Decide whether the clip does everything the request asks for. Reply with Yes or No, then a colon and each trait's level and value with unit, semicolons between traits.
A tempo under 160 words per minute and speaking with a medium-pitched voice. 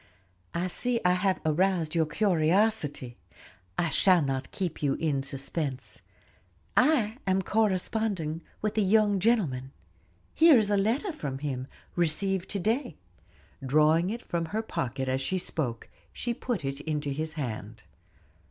Yes: average, 145 wpm; medium, 170 Hz